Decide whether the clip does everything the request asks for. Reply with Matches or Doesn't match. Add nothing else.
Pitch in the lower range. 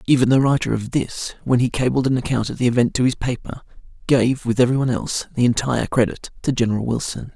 Matches